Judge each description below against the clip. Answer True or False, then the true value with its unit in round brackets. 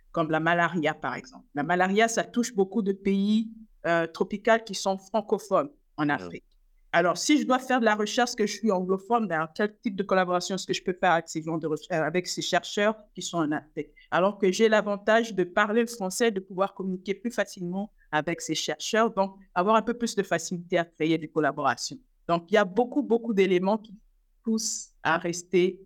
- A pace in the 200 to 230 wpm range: True (205 wpm)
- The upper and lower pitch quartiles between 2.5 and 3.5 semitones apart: False (4.0 semitones)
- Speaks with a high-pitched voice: True (195 Hz)